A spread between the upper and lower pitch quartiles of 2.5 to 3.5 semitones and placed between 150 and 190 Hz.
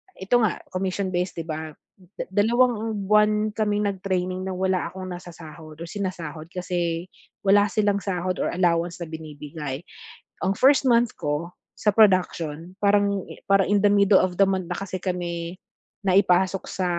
Yes: average, 3.0 semitones; medium, 185 Hz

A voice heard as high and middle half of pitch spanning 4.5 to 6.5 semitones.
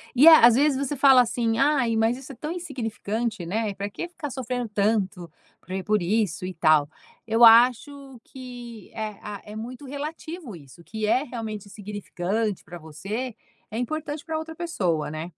Yes: high, 225 Hz; average, 4.8 semitones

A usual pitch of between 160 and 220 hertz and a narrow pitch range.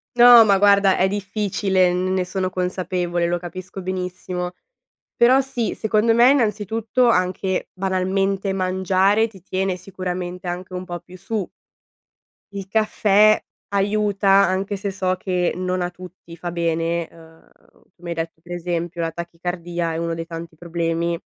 Yes: medium, 185 Hz; narrow, 2.2 semitones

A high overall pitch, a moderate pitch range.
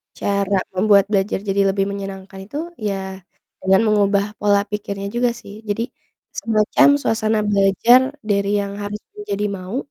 No: high, 205 Hz; narrow, 1.4 semitones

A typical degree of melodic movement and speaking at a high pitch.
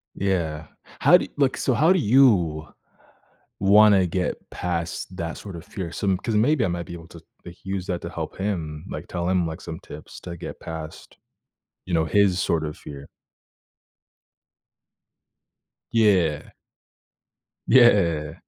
No: average, 3.8 semitones; very low, 90 Hz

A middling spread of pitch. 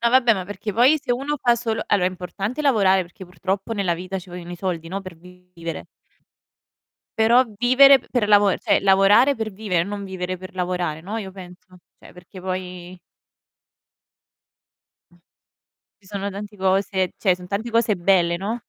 Yes: average, 3.4 semitones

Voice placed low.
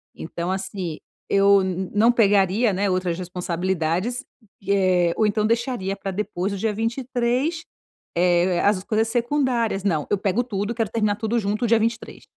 No: high, 205 Hz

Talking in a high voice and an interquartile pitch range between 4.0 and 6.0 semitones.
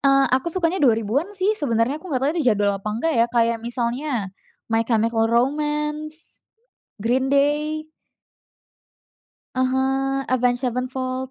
Yes: very high, 260 Hz; average, 4.3 semitones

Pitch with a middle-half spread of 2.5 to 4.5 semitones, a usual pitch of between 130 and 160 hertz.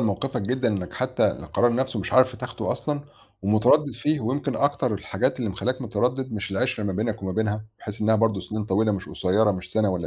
No: average, 4.0 semitones; low, 110 Hz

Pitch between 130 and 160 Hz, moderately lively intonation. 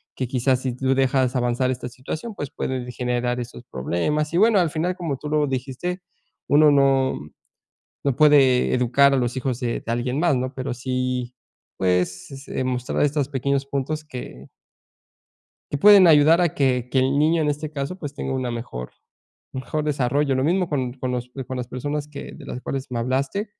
Yes: low, 135 Hz; average, 3.0 semitones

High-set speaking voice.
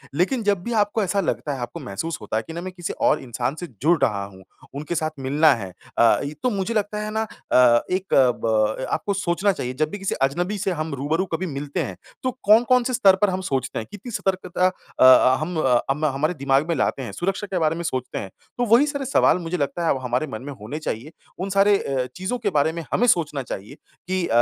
No: medium, 165 Hz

